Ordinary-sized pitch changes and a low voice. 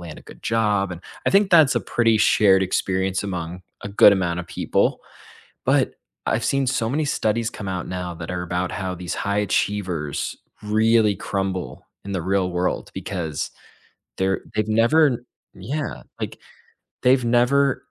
Yes: average, 4.1 semitones; low, 100 Hz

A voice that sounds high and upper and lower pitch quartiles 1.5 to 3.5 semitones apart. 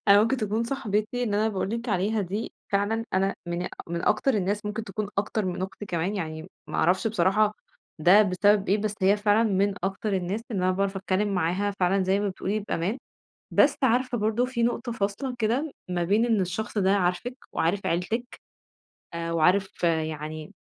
Yes: high, 200 Hz; average, 3.0 semitones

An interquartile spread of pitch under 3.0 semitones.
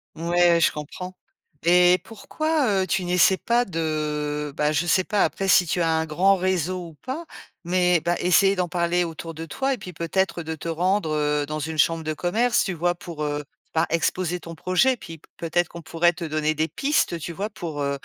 Yes: narrow, 2.6 semitones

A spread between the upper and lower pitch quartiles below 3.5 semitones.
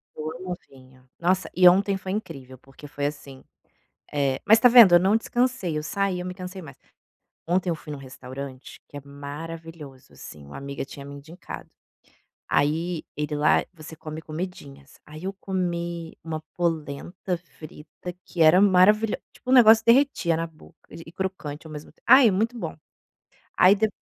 No: average, 4.4 semitones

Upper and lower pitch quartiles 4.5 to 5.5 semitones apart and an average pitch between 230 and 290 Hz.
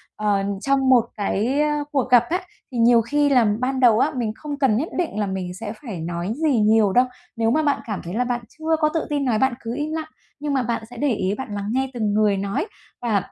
Yes: average, 4.9 semitones; high, 240 Hz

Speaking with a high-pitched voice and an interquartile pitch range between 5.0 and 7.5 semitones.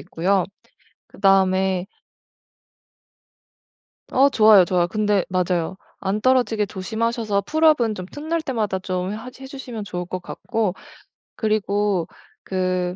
No: high, 200 Hz; average, 3.8 semitones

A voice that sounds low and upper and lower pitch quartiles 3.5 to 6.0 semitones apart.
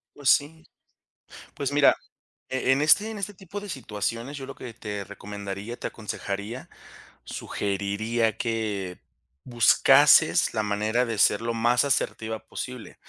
Yes: low, 115 Hz; average, 4.6 semitones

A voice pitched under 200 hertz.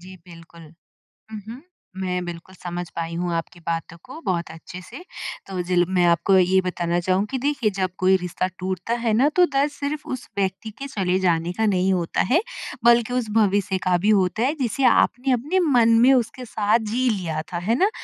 Yes: high, 190 Hz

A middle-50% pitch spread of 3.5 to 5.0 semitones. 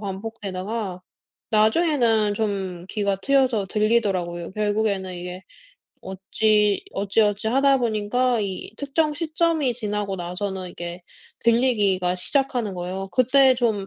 Yes: average, 4.0 semitones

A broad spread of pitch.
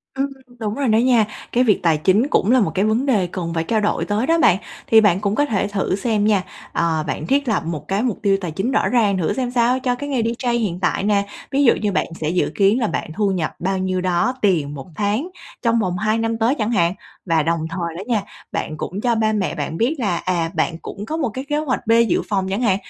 No: average, 4.6 semitones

